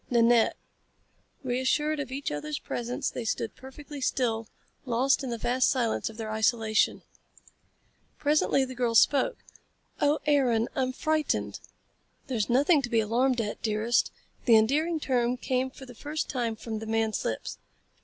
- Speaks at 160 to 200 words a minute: No, average, 150 wpm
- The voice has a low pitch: No, high, 245 Hz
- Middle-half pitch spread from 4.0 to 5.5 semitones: No, average, 3.3 semitones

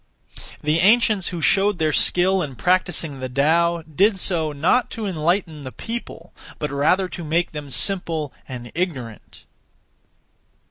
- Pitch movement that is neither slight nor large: Yes, average, 4.1 semitones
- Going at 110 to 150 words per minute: Yes, average, 140 wpm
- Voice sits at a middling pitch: Yes, medium, 170 Hz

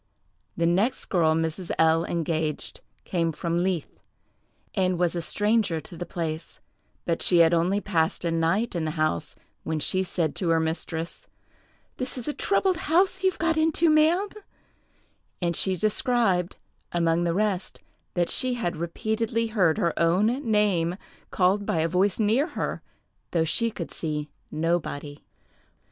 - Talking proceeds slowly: No, average, 155 wpm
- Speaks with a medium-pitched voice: Yes, medium, 175 Hz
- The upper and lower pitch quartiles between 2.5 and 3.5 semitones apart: No, average, 4.8 semitones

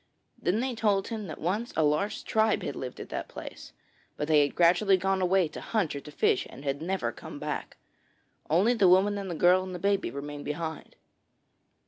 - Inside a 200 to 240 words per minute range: Yes, fast, 205 wpm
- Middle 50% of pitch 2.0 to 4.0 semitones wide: No, average, 4.7 semitones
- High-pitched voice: No, medium, 180 Hz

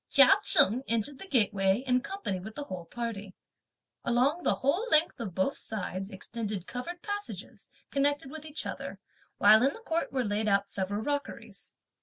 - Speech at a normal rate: Yes, average, 170 wpm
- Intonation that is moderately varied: No, wide, 6.1 semitones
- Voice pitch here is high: Yes, high, 245 Hz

